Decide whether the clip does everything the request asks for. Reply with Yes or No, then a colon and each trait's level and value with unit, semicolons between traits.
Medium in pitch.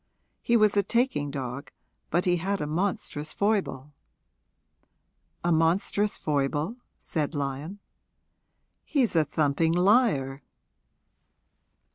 Yes: medium, 165 Hz